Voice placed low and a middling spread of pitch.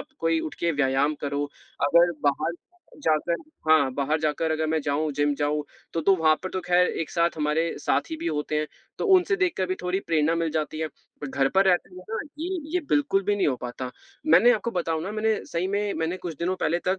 No: medium, 165 Hz; average, 3.8 semitones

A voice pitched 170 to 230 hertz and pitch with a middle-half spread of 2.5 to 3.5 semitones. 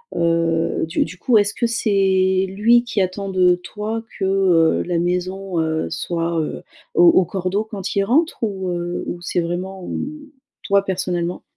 Yes: medium, 185 Hz; average, 2.8 semitones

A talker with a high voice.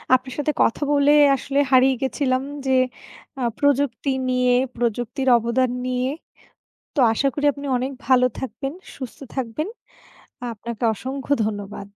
Yes: very high, 260 Hz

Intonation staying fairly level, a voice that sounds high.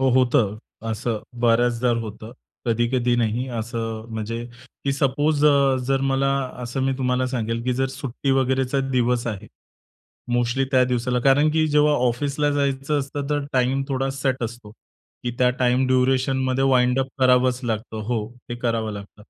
No: narrow, 2.2 semitones; low, 125 Hz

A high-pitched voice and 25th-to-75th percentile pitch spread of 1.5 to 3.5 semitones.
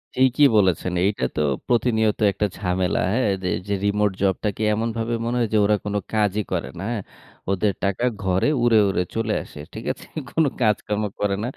No: low, 105 Hz; average, 2.7 semitones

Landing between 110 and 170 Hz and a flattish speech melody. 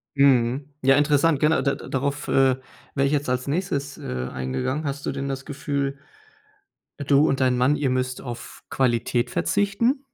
Yes: medium, 140 Hz; narrow, 2.2 semitones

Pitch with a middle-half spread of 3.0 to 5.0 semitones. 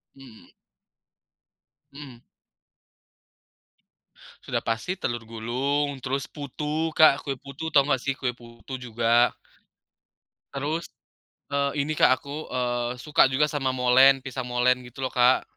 No: narrow, 2.6 semitones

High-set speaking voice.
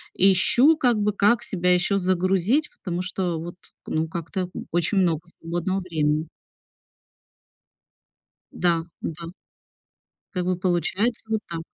No: medium, 180 Hz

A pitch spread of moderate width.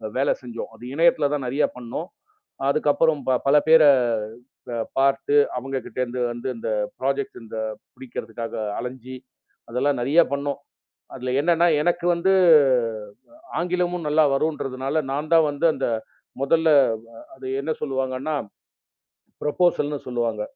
Yes: average, 3.6 semitones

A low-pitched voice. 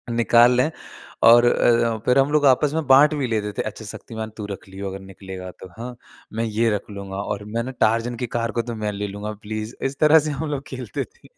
Yes: low, 115 Hz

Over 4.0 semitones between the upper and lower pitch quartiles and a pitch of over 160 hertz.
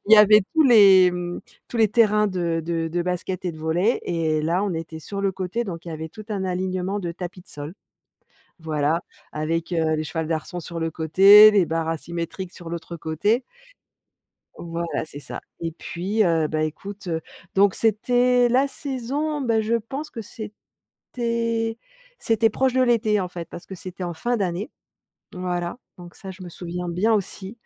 Yes: average, 4.4 semitones; medium, 185 Hz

